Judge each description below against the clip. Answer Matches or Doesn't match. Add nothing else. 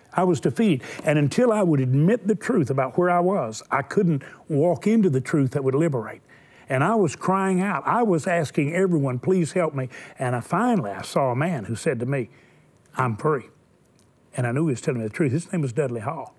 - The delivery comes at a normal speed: Doesn't match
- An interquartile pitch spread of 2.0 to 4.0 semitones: Doesn't match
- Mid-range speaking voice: Matches